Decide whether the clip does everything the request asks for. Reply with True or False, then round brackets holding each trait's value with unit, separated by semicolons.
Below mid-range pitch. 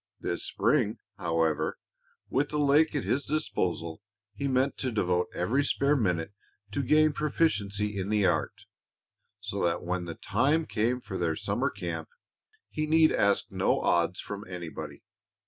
True (105 Hz)